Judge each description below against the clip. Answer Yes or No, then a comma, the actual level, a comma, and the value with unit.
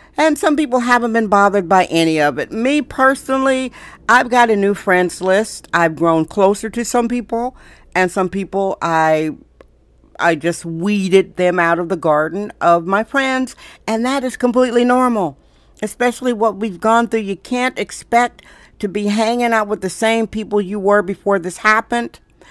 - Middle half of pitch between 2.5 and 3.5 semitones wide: No, average, 4.8 semitones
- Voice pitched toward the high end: Yes, high, 210 Hz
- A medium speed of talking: Yes, average, 175 wpm